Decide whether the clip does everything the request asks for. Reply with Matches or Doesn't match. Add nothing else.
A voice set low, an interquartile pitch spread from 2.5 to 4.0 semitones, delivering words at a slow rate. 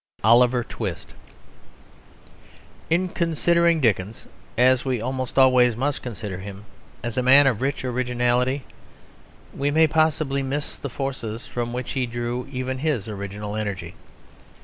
Matches